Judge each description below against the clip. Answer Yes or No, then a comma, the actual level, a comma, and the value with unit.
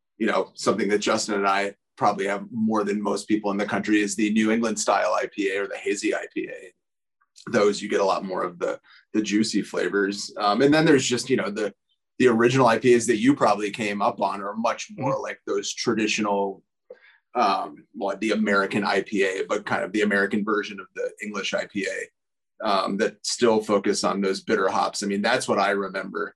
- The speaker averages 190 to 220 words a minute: Yes, fast, 205 wpm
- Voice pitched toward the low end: Yes, low, 105 Hz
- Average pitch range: Yes, average, 3.1 semitones